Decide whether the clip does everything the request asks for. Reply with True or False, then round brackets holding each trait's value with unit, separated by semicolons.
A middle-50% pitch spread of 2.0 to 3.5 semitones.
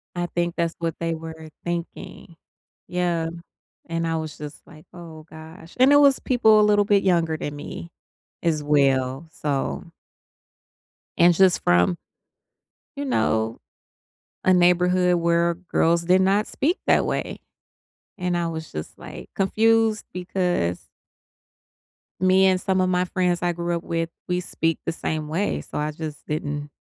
True (2.6 semitones)